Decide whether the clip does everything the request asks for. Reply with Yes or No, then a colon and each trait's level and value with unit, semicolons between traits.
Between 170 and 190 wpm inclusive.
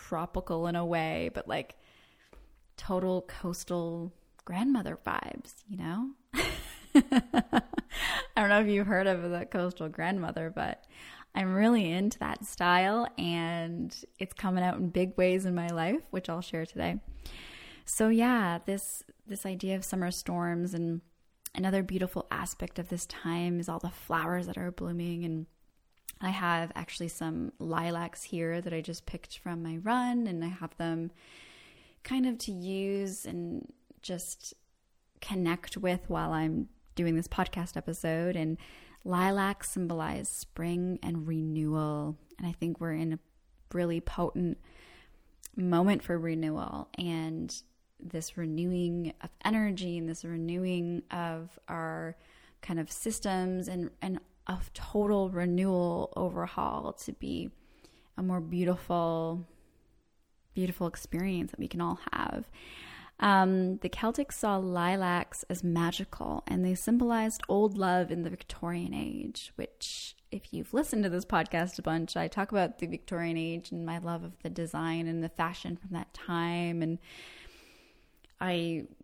No: average, 145 wpm